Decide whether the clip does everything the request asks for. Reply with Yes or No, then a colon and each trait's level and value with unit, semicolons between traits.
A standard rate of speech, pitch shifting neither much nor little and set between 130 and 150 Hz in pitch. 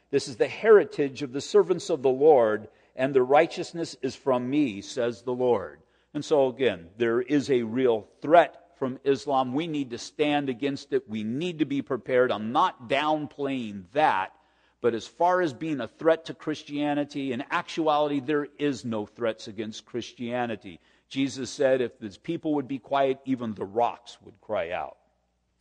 Yes: average, 175 wpm; average, 4.1 semitones; low, 135 Hz